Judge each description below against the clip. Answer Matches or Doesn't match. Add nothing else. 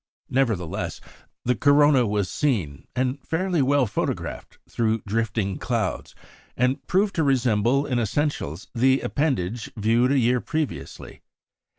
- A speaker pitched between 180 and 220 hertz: Doesn't match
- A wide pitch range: Doesn't match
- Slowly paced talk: Matches